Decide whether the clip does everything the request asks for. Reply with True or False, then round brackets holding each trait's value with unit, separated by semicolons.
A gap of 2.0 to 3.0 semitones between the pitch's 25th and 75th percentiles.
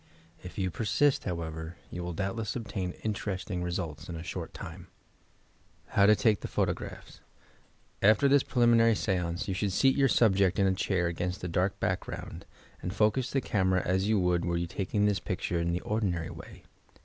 False (3.4 semitones)